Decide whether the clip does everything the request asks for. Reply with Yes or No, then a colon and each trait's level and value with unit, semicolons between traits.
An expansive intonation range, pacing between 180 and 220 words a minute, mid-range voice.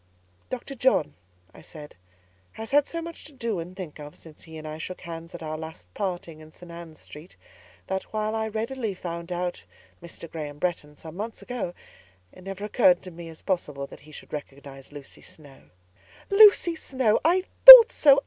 Yes: wide, 6.1 semitones; average, 185 wpm; medium, 175 Hz